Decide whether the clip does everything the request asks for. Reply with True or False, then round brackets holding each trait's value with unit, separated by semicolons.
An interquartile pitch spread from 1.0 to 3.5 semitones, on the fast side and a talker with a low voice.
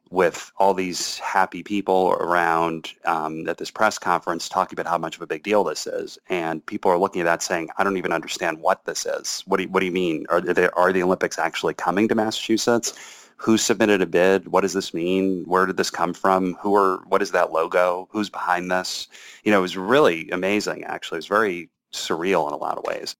True (3.1 semitones; 230 wpm; 95 Hz)